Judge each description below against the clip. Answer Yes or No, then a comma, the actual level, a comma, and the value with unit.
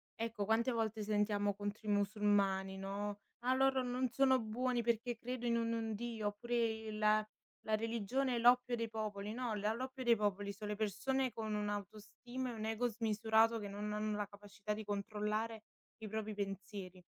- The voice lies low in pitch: No, high, 215 Hz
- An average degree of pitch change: No, narrow, 2.2 semitones